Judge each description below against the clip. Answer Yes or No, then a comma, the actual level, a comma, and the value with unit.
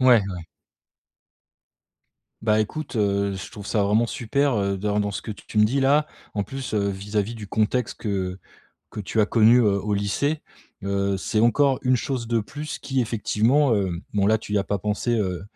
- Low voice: Yes, low, 105 Hz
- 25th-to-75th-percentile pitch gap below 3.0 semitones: No, average, 3.3 semitones